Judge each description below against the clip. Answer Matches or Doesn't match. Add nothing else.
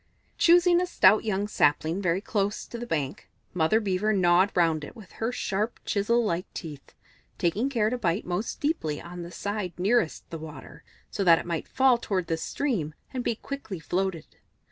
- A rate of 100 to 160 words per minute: Doesn't match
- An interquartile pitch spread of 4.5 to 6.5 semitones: Matches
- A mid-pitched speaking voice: Doesn't match